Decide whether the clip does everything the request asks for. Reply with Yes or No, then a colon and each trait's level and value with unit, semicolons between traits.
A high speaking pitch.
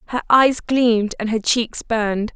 Yes: high, 230 Hz